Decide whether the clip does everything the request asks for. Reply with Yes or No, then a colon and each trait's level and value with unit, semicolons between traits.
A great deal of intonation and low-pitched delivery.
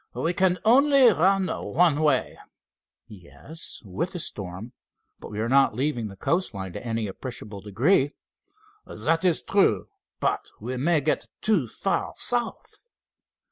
No: wide, 8.8 semitones; medium, 145 Hz